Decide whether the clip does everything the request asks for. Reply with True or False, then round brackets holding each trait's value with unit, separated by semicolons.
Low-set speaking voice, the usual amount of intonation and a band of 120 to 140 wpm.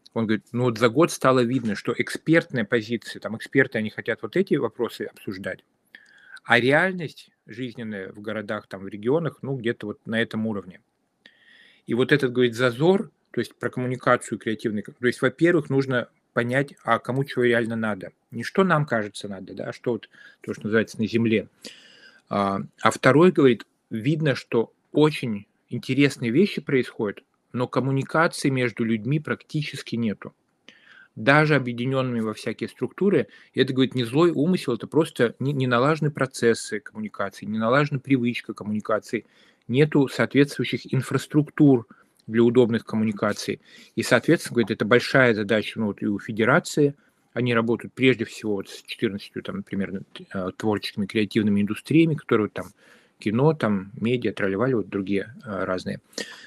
False (120 Hz; 4.1 semitones; 155 wpm)